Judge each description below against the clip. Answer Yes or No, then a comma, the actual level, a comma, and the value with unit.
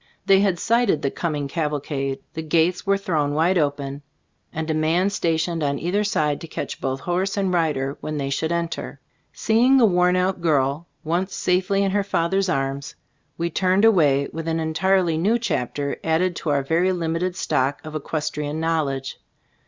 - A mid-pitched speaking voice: Yes, medium, 165 Hz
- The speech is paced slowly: No, average, 175 wpm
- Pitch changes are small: No, average, 3.9 semitones